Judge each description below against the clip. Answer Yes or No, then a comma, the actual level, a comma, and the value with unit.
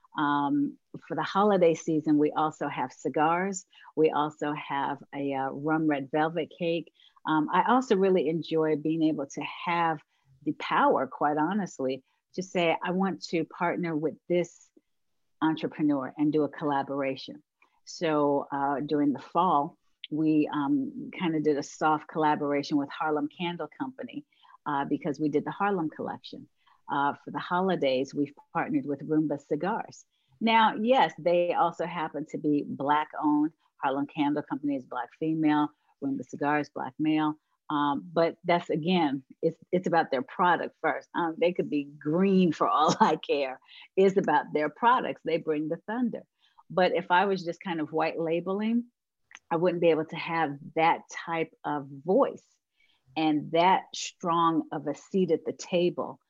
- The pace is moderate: Yes, average, 160 wpm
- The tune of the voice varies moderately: Yes, average, 3.4 semitones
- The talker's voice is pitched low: No, medium, 160 Hz